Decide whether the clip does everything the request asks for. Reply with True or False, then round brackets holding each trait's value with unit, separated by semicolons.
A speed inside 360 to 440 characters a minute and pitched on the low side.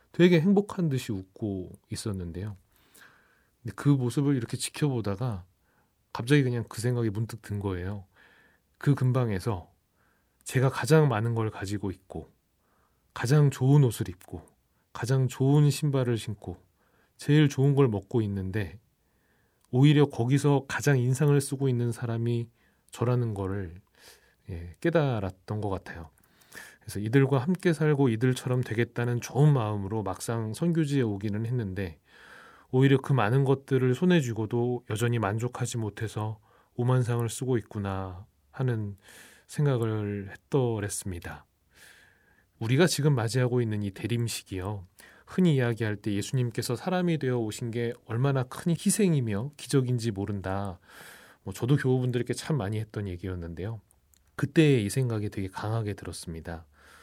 False (295 characters per minute; 115 Hz)